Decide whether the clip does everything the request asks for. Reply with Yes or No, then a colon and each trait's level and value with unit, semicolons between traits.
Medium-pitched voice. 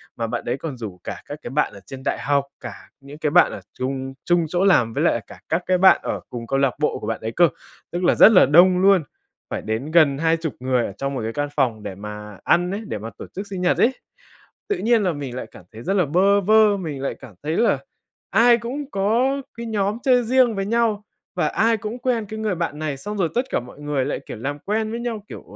Yes: medium, 170 Hz